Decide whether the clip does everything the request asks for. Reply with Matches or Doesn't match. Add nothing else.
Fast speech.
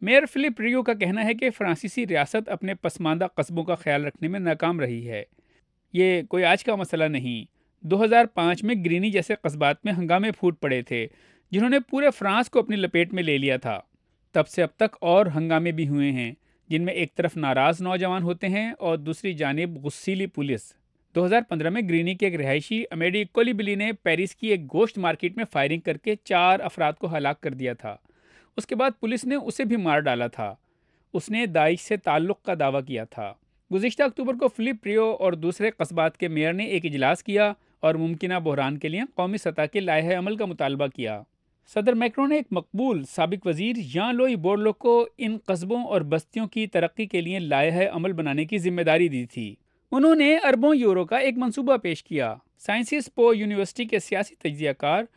Matches